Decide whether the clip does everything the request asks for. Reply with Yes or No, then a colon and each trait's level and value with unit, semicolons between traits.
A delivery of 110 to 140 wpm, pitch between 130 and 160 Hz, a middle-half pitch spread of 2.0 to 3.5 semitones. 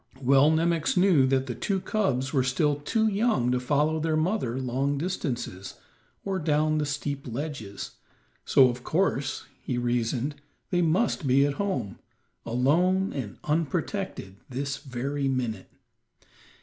No: slow, 135 wpm; medium, 140 Hz; average, 4.5 semitones